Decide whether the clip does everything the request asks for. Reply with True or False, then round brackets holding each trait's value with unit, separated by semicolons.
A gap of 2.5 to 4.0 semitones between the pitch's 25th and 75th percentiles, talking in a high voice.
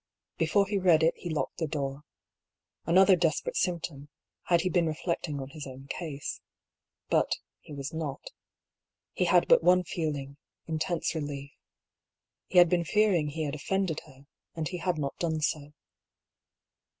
False (3.6 semitones; 160 Hz)